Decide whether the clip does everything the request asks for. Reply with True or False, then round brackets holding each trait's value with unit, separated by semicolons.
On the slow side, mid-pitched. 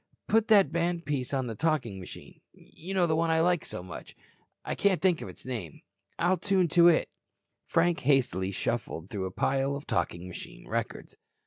False (190 wpm; 150 Hz)